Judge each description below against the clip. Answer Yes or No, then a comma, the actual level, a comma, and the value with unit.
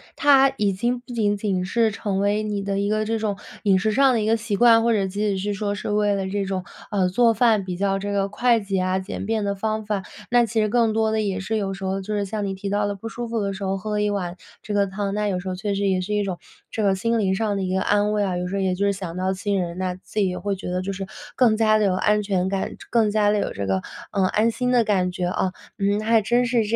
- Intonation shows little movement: Yes, narrow, 2.1 semitones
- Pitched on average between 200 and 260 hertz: Yes, high, 205 Hz